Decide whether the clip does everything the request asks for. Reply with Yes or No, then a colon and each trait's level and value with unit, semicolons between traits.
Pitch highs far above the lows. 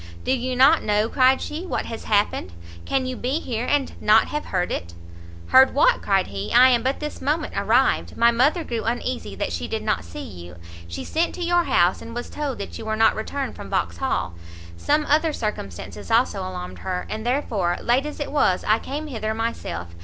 Yes: wide, 6.2 semitones